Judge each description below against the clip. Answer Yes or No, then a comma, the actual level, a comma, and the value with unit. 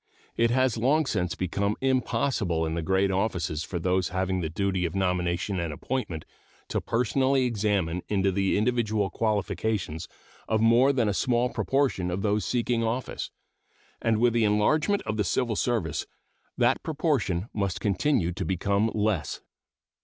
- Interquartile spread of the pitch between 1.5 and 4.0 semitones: No, average, 4.6 semitones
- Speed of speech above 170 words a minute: No, average, 155 wpm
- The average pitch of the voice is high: No, low, 105 Hz